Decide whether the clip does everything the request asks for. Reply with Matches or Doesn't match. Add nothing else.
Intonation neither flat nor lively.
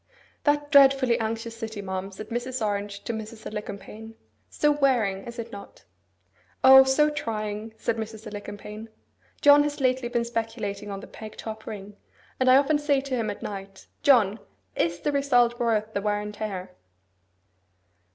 Matches